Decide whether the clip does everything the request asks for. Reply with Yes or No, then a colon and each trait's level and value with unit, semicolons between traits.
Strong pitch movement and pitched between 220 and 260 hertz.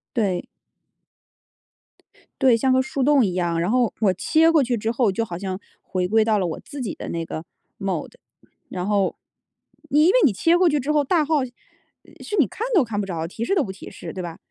Yes: wide, 7.3 semitones; high, 225 Hz